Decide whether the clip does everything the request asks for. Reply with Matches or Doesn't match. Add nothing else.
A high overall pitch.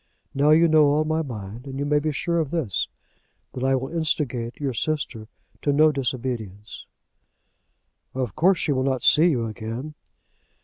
Doesn't match